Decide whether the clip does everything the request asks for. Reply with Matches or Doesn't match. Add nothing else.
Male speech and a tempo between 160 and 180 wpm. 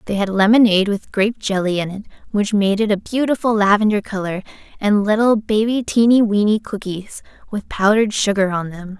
Doesn't match